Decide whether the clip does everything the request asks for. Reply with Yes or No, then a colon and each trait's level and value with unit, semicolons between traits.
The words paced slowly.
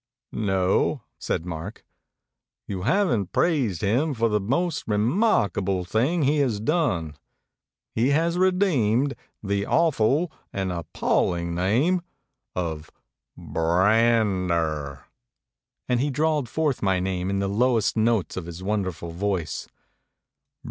Yes: slow, 130 wpm